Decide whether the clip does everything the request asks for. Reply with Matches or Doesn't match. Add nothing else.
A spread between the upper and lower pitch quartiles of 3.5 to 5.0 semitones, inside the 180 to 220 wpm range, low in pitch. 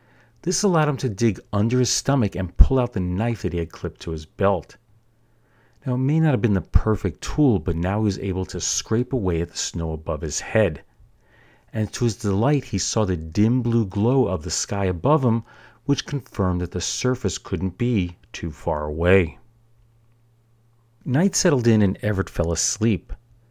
Matches